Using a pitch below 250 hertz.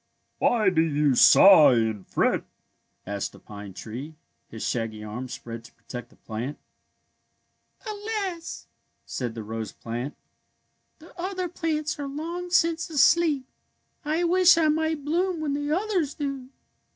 No: very high, 275 Hz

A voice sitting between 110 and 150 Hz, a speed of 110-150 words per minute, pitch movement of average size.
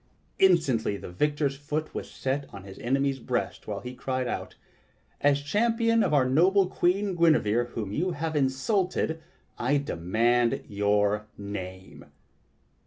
No: low, 135 Hz; slow, 135 wpm; wide, 6.8 semitones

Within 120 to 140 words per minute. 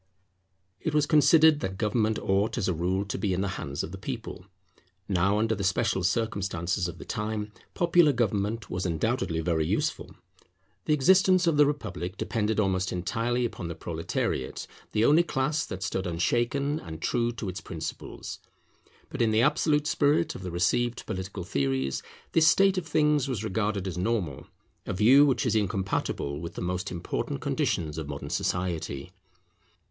No: average, 170 wpm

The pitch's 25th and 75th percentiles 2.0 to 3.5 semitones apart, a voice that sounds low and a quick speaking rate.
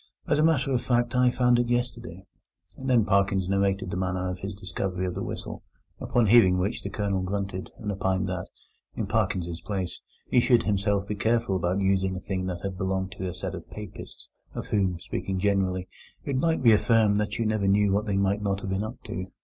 Yes: average, 2.9 semitones; low, 100 Hz; fast, 215 wpm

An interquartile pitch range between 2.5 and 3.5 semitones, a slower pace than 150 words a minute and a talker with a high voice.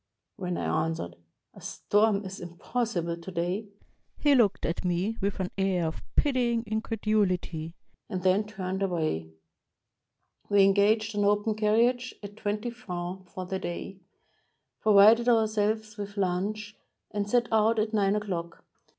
Yes: average, 3.1 semitones; average, 140 wpm; high, 205 Hz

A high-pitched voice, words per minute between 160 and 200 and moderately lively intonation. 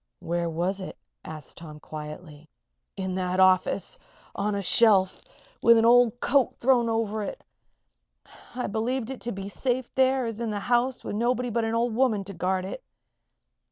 Yes: high, 220 Hz; average, 175 wpm; average, 4.5 semitones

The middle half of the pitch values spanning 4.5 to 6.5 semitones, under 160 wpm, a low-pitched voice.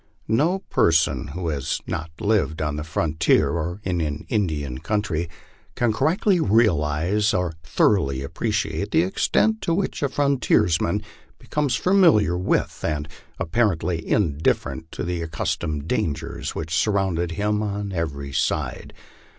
Yes: wide, 5.4 semitones; slow, 135 wpm; very low, 85 Hz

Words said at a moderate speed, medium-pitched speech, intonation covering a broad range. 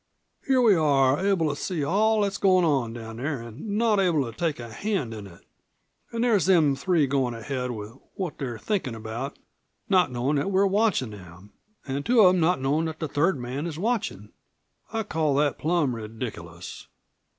Yes: average, 195 wpm; medium, 150 Hz; wide, 7.6 semitones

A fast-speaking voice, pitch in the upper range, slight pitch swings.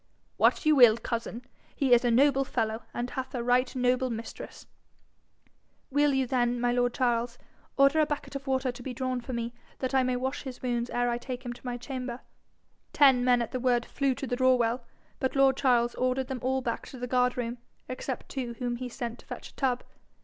Yes: fast, 220 wpm; very high, 250 Hz; narrow, 1.5 semitones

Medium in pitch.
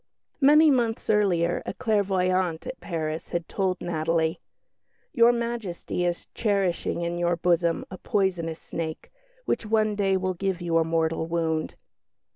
Yes: medium, 180 Hz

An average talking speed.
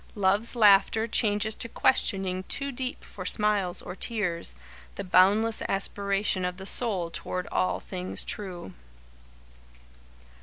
No: slow, 120 wpm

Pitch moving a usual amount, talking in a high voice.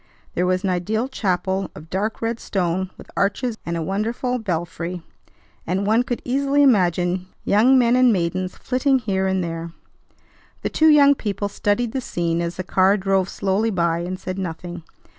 Yes: average, 4.5 semitones; high, 195 Hz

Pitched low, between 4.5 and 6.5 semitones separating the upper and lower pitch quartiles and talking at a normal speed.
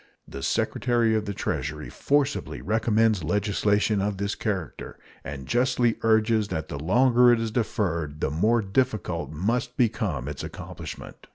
Yes: low, 105 Hz; average, 4.9 semitones; average, 145 wpm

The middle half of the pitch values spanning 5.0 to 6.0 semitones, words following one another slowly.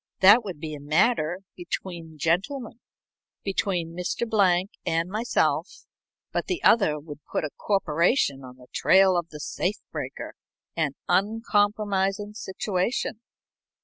No: average, 4.3 semitones; slow, 125 wpm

